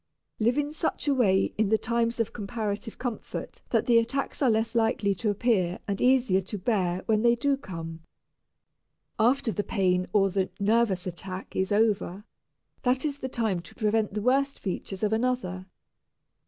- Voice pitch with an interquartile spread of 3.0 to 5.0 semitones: Yes, average, 3.8 semitones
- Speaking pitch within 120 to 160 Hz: No, high, 220 Hz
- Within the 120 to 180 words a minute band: Yes, average, 170 wpm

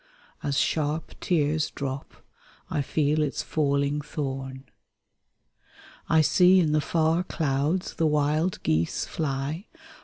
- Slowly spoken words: Yes, slow, 120 wpm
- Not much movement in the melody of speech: Yes, narrow, 2.3 semitones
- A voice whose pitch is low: No, medium, 150 Hz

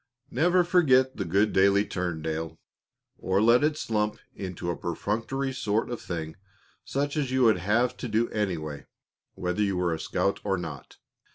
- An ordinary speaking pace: Yes, average, 170 wpm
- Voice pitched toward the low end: Yes, low, 105 Hz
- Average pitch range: No, wide, 6.1 semitones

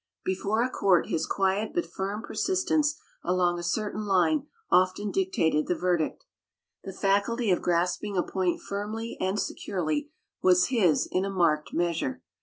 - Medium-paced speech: Yes, average, 150 wpm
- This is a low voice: No, high, 195 Hz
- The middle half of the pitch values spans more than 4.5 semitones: No, average, 3.5 semitones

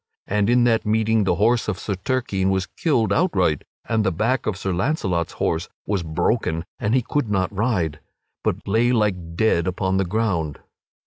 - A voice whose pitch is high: No, low, 100 Hz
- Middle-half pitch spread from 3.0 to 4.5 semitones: Yes, average, 3.7 semitones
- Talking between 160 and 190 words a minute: Yes, average, 180 wpm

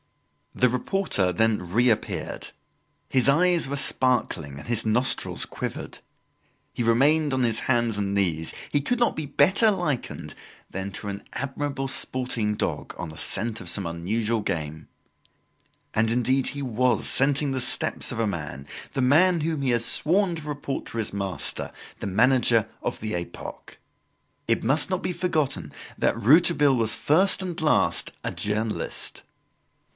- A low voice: Yes, low, 125 Hz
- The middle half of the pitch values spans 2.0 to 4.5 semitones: No, wide, 5.6 semitones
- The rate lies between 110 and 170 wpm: Yes, average, 155 wpm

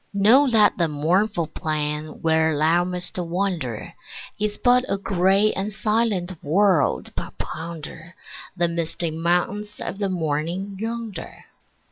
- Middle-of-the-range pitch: Yes, medium, 180 Hz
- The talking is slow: Yes, slow, 125 wpm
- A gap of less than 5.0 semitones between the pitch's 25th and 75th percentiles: Yes, average, 4.3 semitones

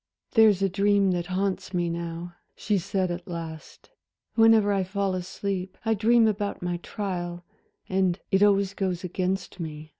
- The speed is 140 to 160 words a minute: Yes, average, 155 wpm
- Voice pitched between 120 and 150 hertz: No, high, 190 Hz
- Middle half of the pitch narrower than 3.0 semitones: Yes, narrow, 2.4 semitones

